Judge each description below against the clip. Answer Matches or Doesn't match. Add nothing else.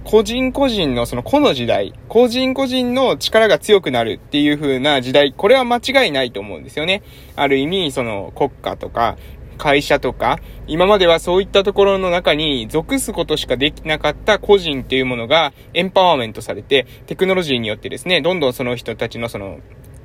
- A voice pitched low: Doesn't match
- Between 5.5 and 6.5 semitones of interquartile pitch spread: Doesn't match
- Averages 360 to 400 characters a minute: Matches